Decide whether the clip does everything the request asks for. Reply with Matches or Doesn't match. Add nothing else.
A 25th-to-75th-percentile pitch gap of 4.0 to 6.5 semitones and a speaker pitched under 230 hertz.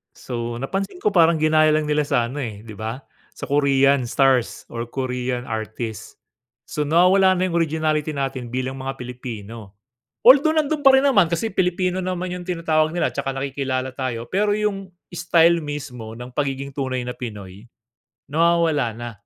Matches